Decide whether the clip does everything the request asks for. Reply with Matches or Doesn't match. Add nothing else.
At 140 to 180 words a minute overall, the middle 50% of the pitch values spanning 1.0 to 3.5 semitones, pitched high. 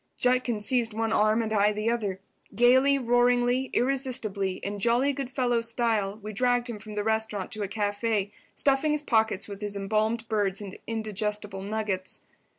Matches